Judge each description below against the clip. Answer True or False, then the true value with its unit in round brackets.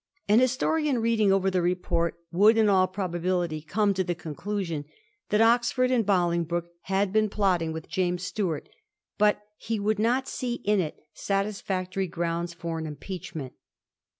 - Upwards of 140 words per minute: True (150 wpm)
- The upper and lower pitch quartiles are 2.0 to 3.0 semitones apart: False (3.6 semitones)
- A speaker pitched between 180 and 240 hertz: True (190 Hz)